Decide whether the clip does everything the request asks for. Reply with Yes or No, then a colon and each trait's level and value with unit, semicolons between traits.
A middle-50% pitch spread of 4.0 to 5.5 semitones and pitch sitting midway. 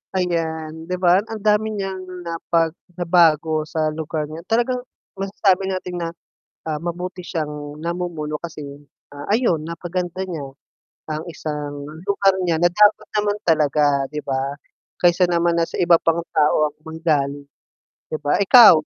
No: average, 3.0 semitones; medium, 170 Hz